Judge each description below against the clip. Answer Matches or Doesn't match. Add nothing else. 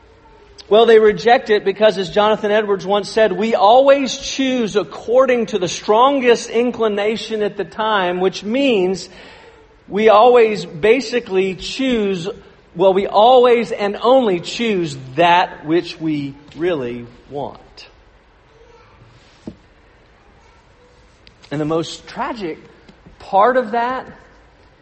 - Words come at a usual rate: Doesn't match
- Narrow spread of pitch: Doesn't match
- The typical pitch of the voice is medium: Doesn't match